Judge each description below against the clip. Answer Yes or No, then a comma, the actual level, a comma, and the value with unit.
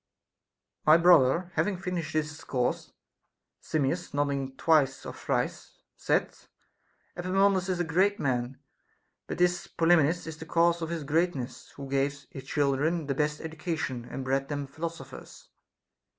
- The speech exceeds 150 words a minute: No, average, 145 wpm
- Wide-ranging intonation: No, average, 3.9 semitones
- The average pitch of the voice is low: No, medium, 155 Hz